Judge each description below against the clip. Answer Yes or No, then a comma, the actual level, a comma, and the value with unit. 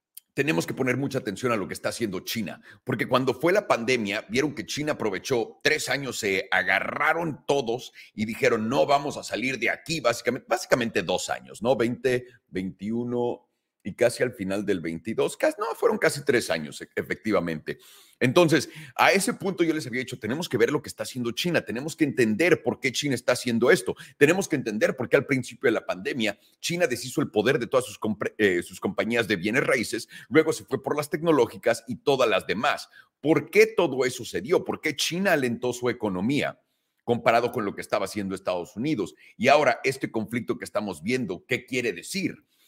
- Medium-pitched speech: No, low, 125 Hz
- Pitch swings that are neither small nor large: No, wide, 5.7 semitones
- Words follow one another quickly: Yes, fast, 200 wpm